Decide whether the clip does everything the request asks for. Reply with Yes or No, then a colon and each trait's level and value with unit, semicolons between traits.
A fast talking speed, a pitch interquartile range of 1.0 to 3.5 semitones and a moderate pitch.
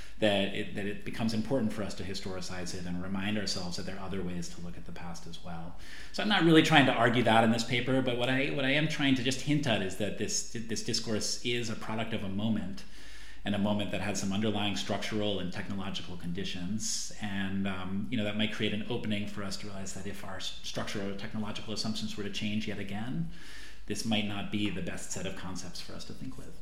No: fast, 245 wpm; narrow, 2.5 semitones; low, 105 Hz